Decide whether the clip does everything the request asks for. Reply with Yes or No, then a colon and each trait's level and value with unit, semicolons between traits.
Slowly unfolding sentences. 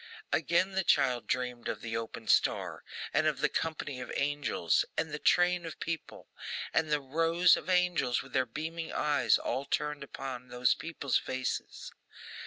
No: average, 165 wpm